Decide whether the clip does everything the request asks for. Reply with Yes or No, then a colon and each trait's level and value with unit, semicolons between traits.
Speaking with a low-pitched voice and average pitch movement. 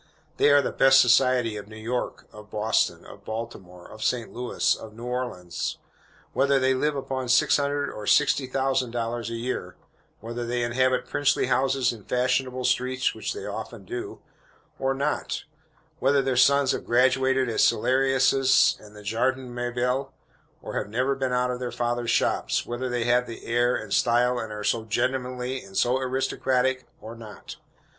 No: low, 125 Hz; narrow, 2.1 semitones